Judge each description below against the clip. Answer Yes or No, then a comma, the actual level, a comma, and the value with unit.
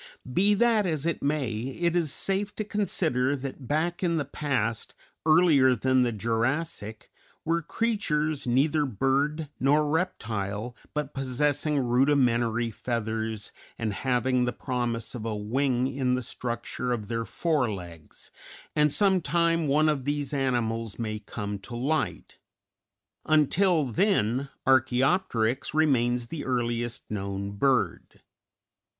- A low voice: Yes, low, 130 Hz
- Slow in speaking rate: Yes, slow, 130 wpm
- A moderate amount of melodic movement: Yes, average, 4.6 semitones